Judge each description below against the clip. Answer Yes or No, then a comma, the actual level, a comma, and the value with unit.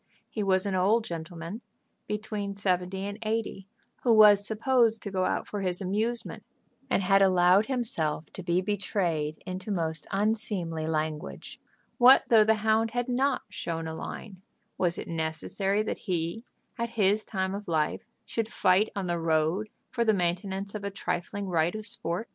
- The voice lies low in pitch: No, high, 195 Hz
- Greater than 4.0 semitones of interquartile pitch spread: No, average, 3.7 semitones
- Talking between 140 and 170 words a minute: Yes, average, 165 wpm